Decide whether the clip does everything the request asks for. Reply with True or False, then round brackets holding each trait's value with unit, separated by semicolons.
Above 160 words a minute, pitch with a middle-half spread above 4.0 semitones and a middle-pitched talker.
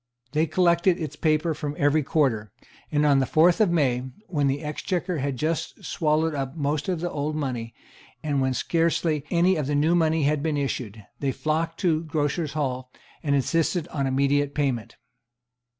False (175 wpm; 2.8 semitones; 150 Hz)